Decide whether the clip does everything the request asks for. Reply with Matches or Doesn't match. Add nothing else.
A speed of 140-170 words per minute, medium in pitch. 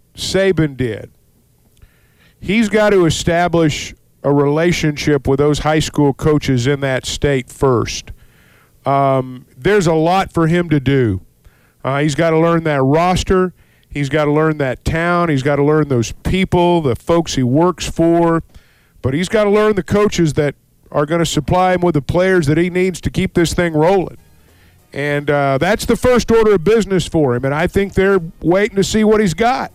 Doesn't match